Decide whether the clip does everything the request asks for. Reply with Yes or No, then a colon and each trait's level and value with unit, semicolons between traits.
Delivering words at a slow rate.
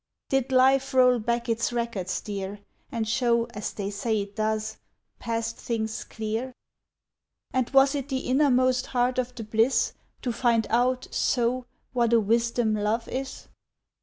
No: average, 150 wpm